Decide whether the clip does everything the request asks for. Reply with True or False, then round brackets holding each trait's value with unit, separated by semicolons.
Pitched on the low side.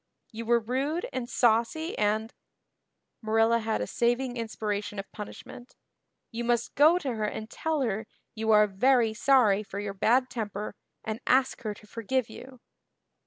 False (230 Hz)